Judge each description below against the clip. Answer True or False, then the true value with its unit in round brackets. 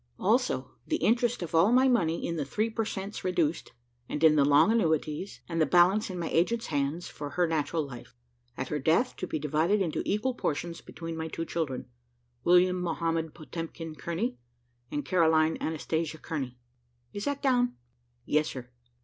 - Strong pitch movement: False (3.8 semitones)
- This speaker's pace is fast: False (175 wpm)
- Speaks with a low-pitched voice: False (165 Hz)